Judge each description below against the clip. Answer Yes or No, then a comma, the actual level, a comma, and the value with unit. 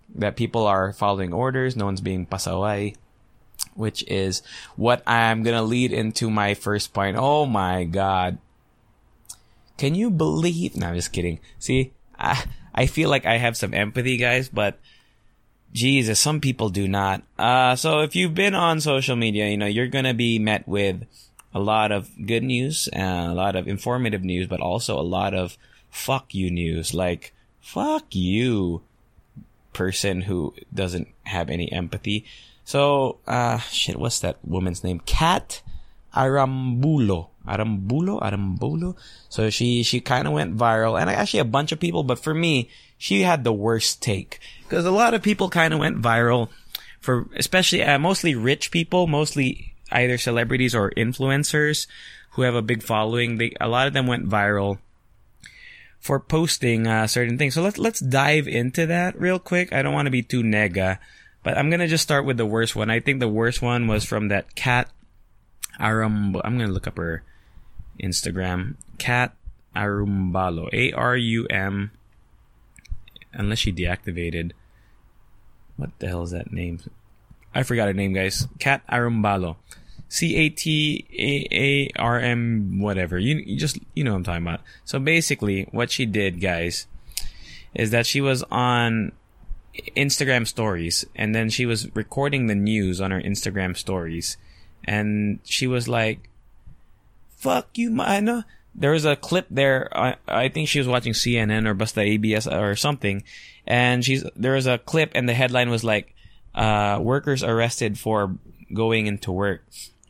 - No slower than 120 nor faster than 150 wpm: No, average, 165 wpm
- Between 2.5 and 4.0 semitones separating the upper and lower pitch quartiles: No, average, 5.0 semitones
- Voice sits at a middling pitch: No, low, 115 Hz